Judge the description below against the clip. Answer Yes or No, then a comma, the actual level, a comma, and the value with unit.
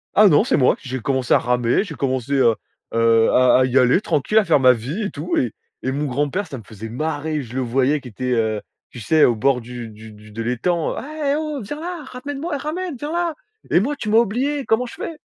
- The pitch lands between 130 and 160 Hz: Yes, medium, 140 Hz